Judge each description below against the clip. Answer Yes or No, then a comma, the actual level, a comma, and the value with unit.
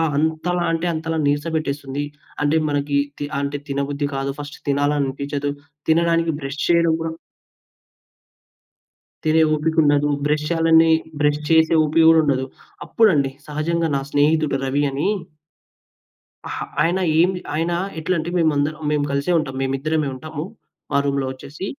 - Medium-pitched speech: Yes, medium, 150 Hz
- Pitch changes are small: Yes, narrow, 2.3 semitones